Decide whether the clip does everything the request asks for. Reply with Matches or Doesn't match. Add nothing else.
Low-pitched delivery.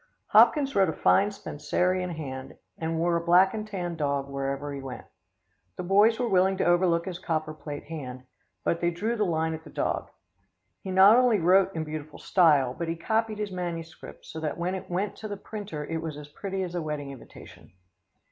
Doesn't match